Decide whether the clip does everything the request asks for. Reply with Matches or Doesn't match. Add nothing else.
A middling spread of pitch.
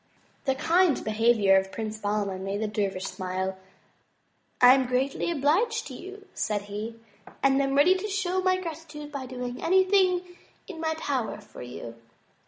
Doesn't match